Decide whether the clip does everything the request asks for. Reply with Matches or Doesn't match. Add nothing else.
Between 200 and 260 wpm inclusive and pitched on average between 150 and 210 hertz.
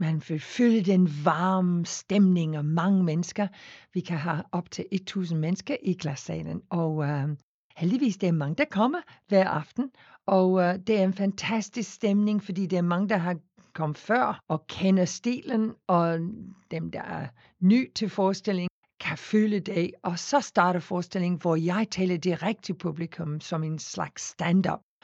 Doesn't match